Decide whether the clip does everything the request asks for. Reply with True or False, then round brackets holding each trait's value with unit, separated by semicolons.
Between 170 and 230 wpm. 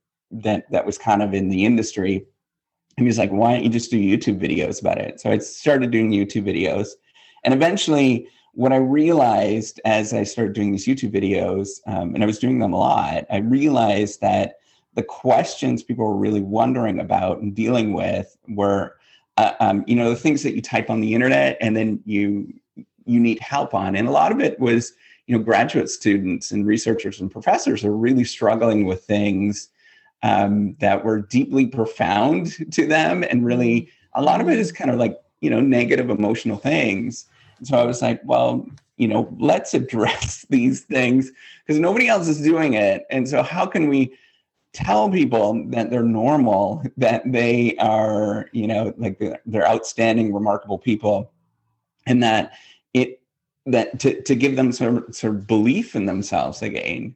True (185 wpm)